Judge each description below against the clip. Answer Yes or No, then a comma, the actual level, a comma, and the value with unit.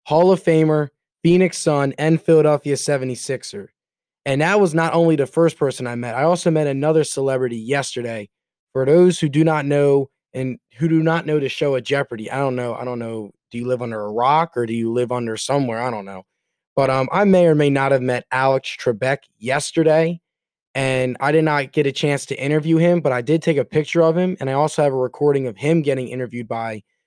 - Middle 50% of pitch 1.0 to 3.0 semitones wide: No, average, 3.9 semitones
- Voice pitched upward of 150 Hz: No, medium, 140 Hz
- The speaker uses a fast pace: Yes, fast, 225 wpm